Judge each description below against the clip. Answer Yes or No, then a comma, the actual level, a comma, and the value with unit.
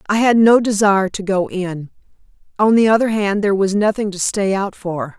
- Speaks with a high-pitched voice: Yes, high, 200 Hz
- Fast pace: Yes, fast, 210 wpm